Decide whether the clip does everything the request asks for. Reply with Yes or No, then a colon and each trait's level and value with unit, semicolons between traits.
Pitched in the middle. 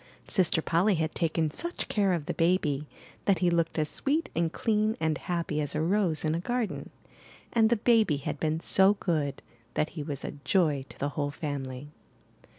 Yes: medium, 165 Hz